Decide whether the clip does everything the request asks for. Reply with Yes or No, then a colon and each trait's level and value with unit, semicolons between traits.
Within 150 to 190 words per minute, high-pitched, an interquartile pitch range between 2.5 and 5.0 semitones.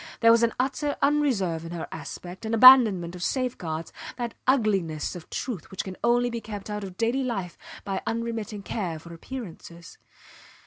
No: average, 170 wpm; high, 215 Hz; wide, 5.4 semitones